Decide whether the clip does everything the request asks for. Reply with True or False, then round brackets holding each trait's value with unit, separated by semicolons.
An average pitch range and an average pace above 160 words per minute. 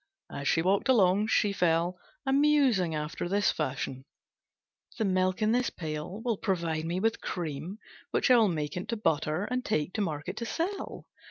False (5.7 semitones; 175 wpm)